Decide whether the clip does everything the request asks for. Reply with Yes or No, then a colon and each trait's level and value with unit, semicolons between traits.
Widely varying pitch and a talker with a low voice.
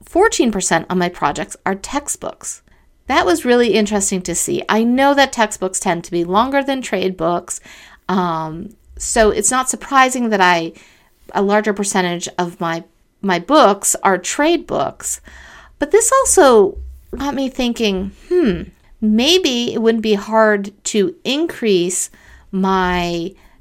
No: wide, 6.4 semitones; high, 205 Hz